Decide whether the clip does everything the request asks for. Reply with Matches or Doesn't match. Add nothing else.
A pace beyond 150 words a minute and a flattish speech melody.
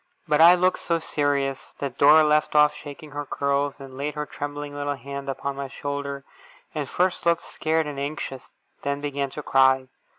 Matches